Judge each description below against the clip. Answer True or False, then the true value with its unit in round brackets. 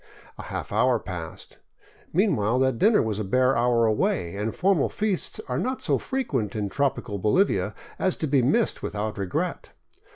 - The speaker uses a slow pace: False (165 wpm)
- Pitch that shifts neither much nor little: False (7.9 semitones)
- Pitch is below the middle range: True (125 Hz)